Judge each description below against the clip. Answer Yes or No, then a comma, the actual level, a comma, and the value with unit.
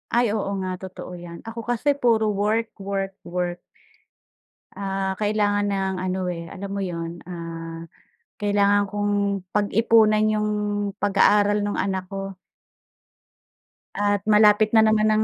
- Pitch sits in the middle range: No, high, 205 Hz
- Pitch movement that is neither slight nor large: No, narrow, 2.0 semitones